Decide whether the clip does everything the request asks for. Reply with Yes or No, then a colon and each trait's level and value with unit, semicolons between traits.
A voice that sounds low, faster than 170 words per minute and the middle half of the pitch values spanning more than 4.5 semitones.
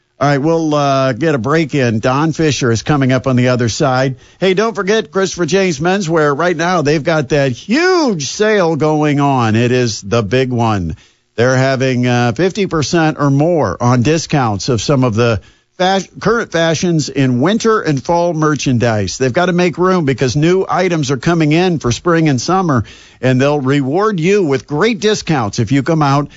No: medium, 150 Hz; average, 190 wpm; average, 5.3 semitones